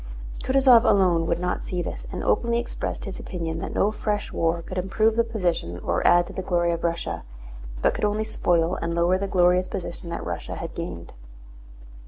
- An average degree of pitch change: Yes, average, 3.6 semitones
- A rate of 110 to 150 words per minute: No, average, 195 wpm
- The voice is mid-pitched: Yes, medium, 180 Hz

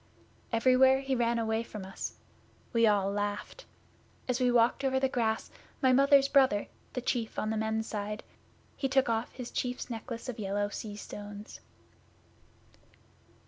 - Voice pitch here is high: Yes, high, 230 Hz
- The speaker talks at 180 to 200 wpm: No, average, 150 wpm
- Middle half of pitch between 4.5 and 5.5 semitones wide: No, average, 3.5 semitones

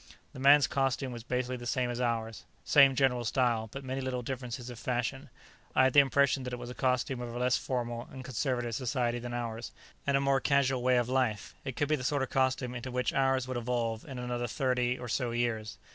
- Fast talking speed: Yes, fast, 230 wpm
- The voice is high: No, low, 125 Hz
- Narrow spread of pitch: Yes, narrow, 1.6 semitones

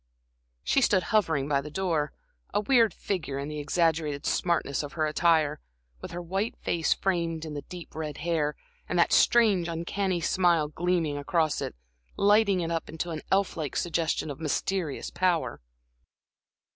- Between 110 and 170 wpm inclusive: Yes, average, 160 wpm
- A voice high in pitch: No, medium, 165 Hz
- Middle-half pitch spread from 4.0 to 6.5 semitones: No, average, 3.2 semitones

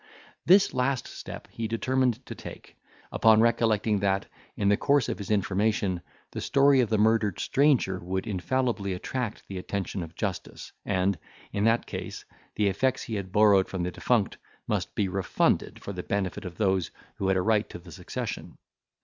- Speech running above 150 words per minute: Yes, average, 175 wpm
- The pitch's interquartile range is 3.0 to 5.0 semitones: Yes, average, 3.4 semitones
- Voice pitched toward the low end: Yes, low, 105 Hz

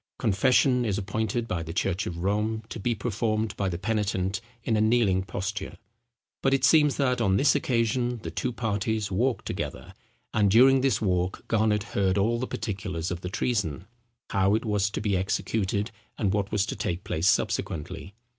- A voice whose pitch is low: Yes, low, 105 Hz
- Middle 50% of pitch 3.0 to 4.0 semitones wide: Yes, average, 3.3 semitones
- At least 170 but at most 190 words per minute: Yes, average, 175 wpm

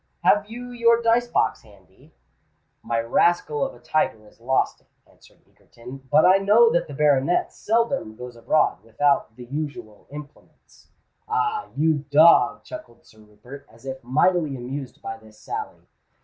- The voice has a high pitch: No, medium, 145 Hz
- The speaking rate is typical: Yes, average, 155 wpm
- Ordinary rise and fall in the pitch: No, wide, 8.5 semitones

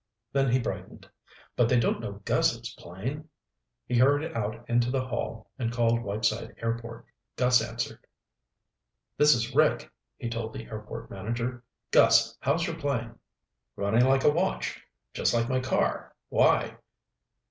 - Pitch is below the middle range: Yes, low, 120 Hz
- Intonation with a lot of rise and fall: No, narrow, 2.6 semitones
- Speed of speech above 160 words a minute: No, average, 145 wpm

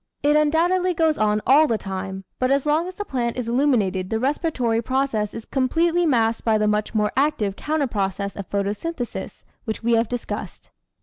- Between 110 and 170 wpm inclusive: No, average, 185 wpm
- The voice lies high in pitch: Yes, high, 240 Hz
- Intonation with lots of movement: Yes, wide, 5.9 semitones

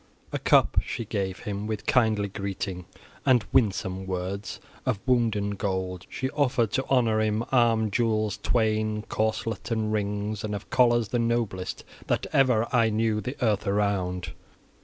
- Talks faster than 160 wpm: No, average, 155 wpm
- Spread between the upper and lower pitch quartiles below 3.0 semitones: Yes, narrow, 2.6 semitones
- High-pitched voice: No, low, 110 Hz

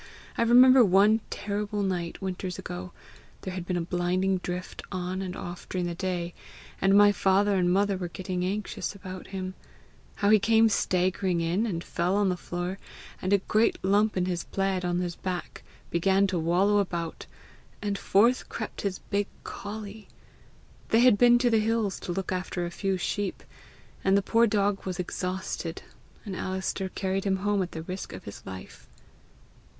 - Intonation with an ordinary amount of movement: No, narrow, 2.2 semitones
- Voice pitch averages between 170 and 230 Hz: Yes, high, 190 Hz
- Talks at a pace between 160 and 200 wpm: Yes, average, 175 wpm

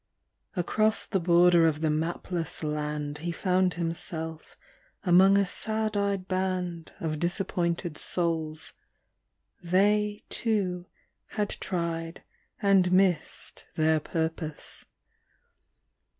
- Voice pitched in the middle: Yes, medium, 175 Hz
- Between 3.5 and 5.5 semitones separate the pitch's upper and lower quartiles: No, average, 2.8 semitones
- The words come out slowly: Yes, slow, 95 wpm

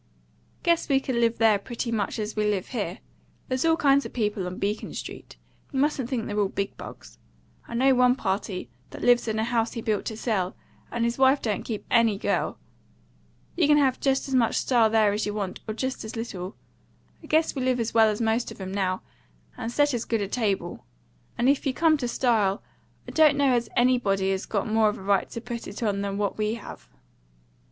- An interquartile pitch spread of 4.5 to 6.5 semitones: No, average, 3.8 semitones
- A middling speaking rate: No, fast, 225 wpm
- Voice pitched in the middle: No, high, 230 Hz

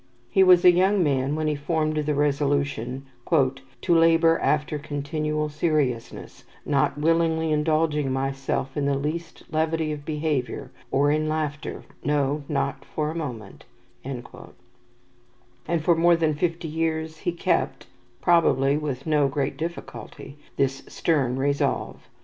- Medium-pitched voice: Yes, medium, 150 Hz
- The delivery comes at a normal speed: No, slow, 130 wpm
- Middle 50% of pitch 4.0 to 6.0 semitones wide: No, average, 2.8 semitones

